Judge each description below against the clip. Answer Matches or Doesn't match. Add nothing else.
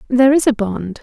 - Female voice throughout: Matches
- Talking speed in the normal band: Doesn't match